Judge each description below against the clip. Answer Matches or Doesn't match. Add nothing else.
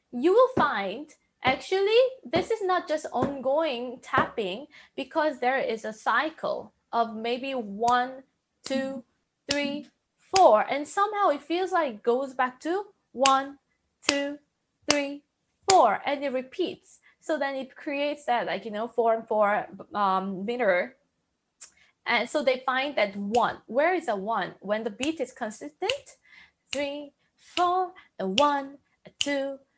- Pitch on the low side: Doesn't match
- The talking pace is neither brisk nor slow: Matches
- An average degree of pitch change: Matches